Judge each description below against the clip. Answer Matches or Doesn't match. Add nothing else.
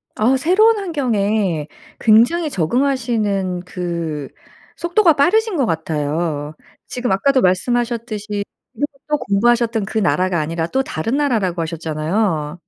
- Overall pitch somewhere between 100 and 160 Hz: Doesn't match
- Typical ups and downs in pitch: Doesn't match